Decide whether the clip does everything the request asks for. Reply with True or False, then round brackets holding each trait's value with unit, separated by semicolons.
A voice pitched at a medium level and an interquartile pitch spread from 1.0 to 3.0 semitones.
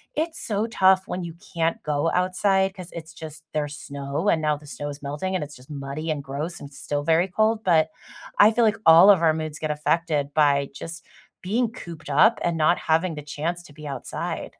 False (160 Hz; 3.8 semitones)